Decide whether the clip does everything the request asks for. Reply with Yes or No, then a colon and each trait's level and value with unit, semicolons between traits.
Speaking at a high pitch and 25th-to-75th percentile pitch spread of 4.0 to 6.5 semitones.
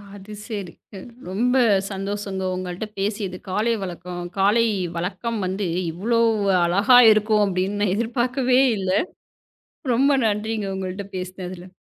No: high, 200 Hz; average, 3.2 semitones